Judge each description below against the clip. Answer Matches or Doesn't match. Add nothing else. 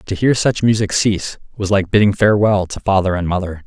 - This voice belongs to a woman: Doesn't match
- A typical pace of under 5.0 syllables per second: Doesn't match